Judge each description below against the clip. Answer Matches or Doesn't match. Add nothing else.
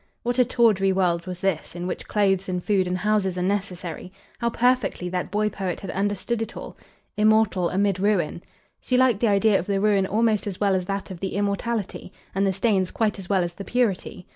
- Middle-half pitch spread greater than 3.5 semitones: Doesn't match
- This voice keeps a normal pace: Doesn't match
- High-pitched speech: Matches